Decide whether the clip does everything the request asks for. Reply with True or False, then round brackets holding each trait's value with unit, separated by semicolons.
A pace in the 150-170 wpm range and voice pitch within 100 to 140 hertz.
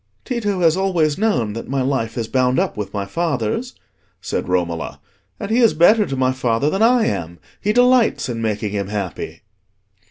False (185 wpm; 135 Hz)